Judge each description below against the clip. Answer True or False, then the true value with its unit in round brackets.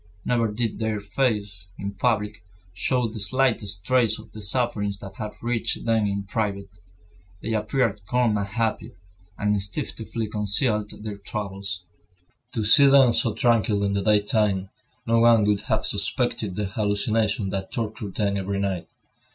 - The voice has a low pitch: True (105 Hz)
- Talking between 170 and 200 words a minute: False (150 wpm)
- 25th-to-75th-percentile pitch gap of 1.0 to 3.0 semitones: True (2.4 semitones)